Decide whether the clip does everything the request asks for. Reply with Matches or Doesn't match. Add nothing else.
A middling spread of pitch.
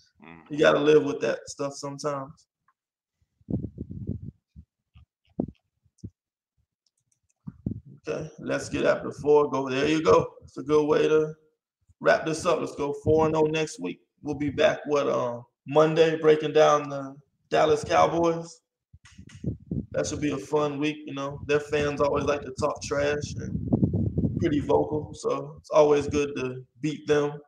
Doesn't match